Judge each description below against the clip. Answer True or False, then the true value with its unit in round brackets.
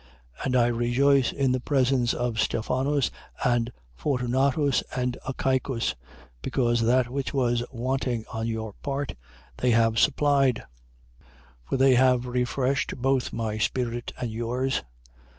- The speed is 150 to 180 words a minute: False (135 wpm)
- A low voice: True (125 Hz)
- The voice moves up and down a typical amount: False (2.1 semitones)